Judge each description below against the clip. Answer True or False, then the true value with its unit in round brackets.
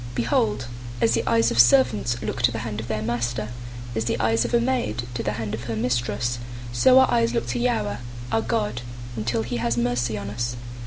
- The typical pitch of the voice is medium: False (120 Hz)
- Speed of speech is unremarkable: False (220 wpm)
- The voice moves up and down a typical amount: False (1.6 semitones)